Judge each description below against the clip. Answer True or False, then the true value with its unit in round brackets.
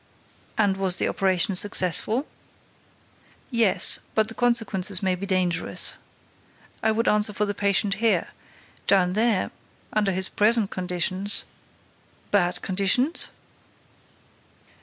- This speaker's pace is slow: True (105 wpm)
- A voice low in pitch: False (200 Hz)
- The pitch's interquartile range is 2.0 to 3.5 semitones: True (2.7 semitones)